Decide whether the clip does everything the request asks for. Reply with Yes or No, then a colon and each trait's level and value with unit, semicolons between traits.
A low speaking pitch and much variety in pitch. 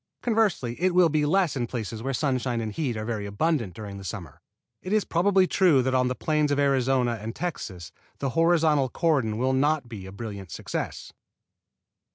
Yes: low, 130 Hz; wide, 6.2 semitones